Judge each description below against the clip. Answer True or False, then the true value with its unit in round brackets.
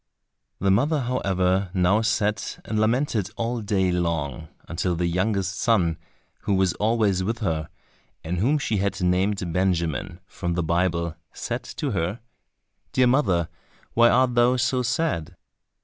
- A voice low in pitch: True (95 Hz)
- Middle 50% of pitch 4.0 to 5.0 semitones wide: True (4.6 semitones)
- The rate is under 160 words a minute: True (145 wpm)